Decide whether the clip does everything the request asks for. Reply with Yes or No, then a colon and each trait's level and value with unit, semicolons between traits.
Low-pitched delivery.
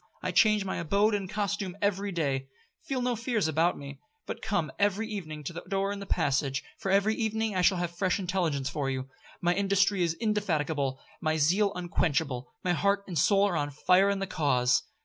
No: medium, 185 Hz